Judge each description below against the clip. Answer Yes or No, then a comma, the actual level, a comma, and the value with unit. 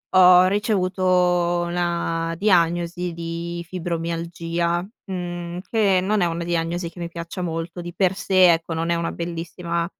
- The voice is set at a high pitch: No, medium, 175 Hz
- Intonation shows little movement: Yes, narrow, 1.3 semitones